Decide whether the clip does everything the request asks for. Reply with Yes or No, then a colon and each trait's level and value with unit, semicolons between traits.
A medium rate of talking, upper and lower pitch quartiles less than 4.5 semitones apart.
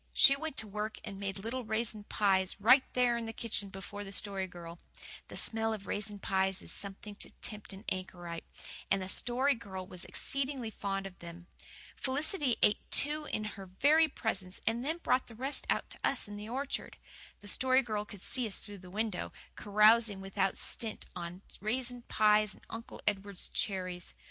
Yes: average, 185 wpm; average, 3.8 semitones